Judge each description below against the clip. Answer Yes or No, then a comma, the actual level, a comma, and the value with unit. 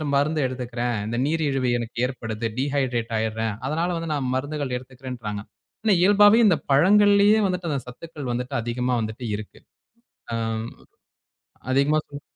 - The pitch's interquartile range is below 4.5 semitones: No, average, 4.9 semitones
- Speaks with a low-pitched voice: Yes, low, 130 Hz